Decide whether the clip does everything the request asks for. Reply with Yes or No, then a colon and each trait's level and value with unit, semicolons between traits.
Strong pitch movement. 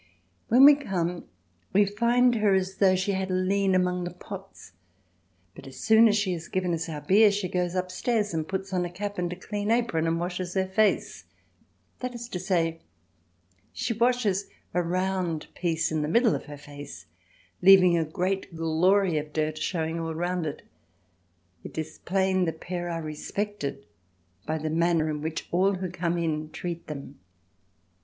No: average, 3.2 semitones